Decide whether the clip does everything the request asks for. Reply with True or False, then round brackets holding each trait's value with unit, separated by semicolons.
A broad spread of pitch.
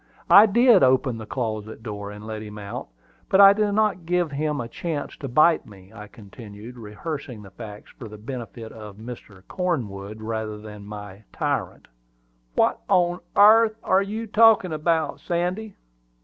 True (9.0 semitones)